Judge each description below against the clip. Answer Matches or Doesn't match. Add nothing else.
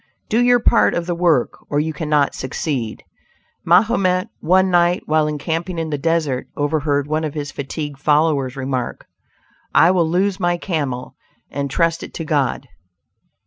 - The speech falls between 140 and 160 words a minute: Matches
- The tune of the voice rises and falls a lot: Doesn't match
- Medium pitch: Matches